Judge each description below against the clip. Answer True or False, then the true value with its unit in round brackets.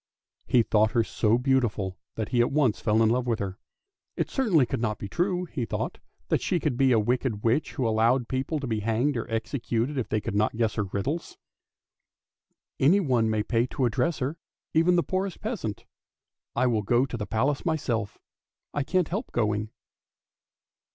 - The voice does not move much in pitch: False (4.8 semitones)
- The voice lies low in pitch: True (120 Hz)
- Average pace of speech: True (190 wpm)